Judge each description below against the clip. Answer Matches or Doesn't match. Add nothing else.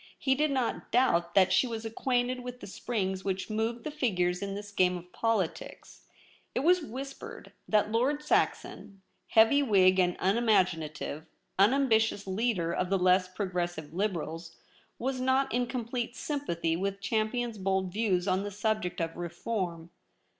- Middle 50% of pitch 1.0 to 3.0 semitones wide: Doesn't match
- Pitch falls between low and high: Doesn't match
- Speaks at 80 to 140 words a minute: Doesn't match